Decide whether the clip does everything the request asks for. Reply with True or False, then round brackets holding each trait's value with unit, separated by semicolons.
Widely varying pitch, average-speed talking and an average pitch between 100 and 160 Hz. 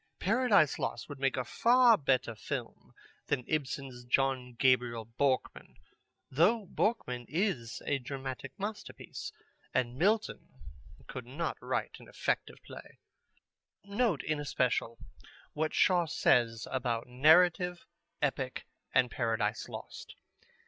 False (6.3 semitones; 115 wpm; 135 Hz)